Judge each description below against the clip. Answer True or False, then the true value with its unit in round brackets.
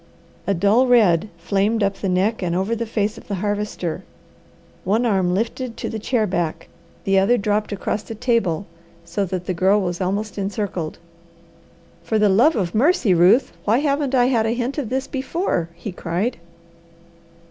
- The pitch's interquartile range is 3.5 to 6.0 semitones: True (3.8 semitones)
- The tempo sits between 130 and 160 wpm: False (175 wpm)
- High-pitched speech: True (205 Hz)